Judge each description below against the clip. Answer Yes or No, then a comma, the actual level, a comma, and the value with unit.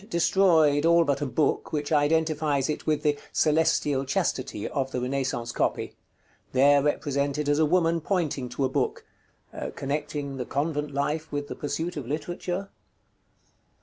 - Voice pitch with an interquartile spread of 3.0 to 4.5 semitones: No, narrow, 2.4 semitones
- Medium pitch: Yes, medium, 145 Hz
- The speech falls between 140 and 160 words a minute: Yes, average, 150 wpm